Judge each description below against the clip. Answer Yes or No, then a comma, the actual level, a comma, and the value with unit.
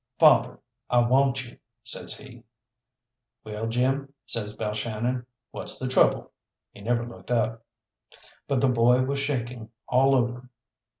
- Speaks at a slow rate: Yes, slow, 130 wpm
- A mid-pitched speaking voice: No, low, 120 Hz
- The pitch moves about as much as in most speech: No, narrow, 2.1 semitones